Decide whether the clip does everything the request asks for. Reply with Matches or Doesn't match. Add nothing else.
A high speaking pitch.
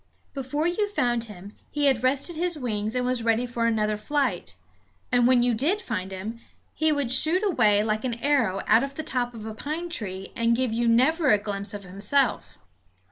Matches